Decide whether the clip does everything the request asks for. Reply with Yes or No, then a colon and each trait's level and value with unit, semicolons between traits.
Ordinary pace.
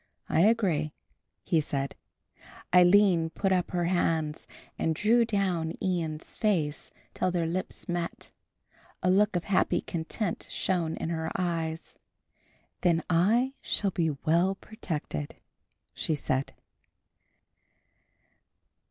No: slow, 110 wpm